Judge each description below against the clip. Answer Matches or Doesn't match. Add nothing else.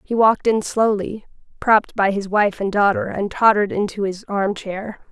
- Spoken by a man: Doesn't match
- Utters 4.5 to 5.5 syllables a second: Matches